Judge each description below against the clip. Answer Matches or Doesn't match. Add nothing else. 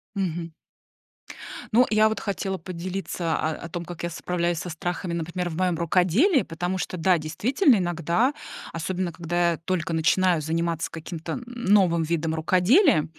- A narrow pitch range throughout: Matches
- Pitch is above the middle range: Doesn't match